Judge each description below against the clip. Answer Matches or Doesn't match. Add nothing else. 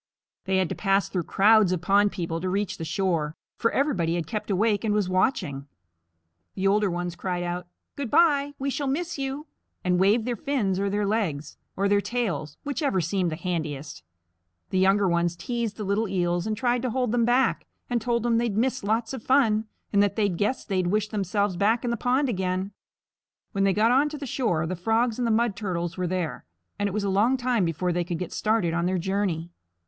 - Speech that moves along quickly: Matches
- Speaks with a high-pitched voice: Matches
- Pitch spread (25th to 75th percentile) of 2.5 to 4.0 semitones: Doesn't match